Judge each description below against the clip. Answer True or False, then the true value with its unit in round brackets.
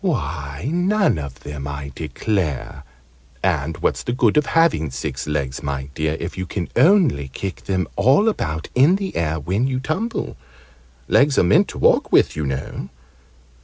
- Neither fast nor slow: True (165 wpm)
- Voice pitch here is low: True (85 Hz)